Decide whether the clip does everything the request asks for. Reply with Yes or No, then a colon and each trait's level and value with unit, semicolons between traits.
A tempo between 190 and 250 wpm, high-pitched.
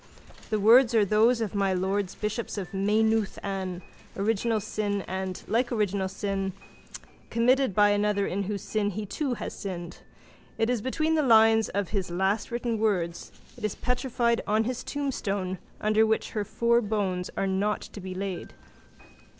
No: average, 165 wpm; high, 210 Hz